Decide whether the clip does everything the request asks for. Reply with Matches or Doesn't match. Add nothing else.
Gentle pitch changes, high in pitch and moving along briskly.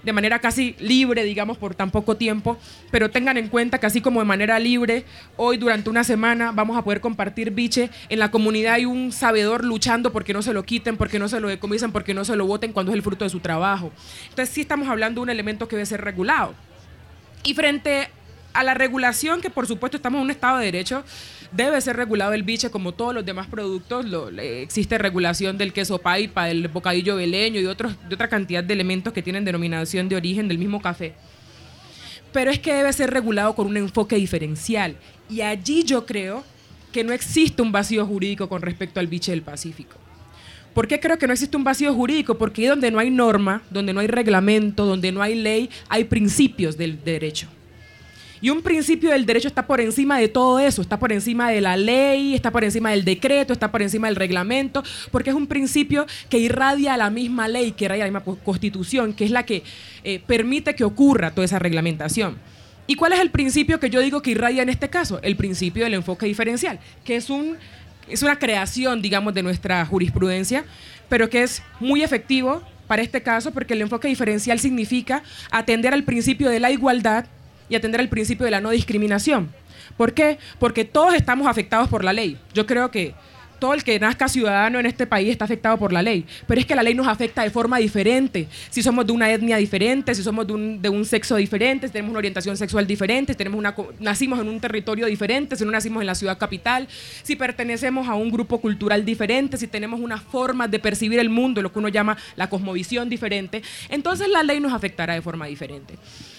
Doesn't match